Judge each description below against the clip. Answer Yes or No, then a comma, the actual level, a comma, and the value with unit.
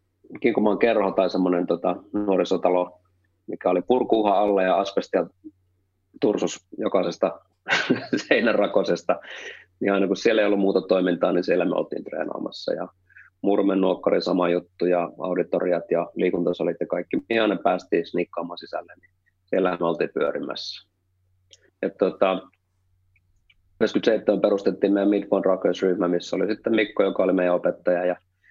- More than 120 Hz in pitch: No, very low, 95 Hz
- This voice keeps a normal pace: Yes, average, 140 wpm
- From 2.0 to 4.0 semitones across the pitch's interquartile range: No, narrow, 1.1 semitones